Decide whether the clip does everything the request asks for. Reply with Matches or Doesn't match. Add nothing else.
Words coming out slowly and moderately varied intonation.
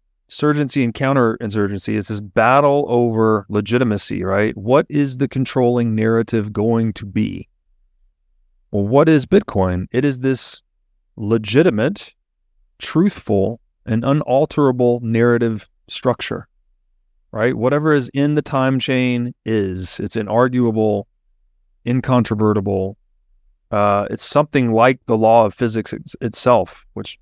Matches